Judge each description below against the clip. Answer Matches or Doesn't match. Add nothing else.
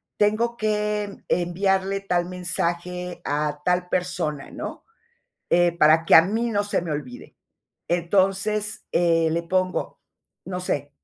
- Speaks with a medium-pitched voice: Matches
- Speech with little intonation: Doesn't match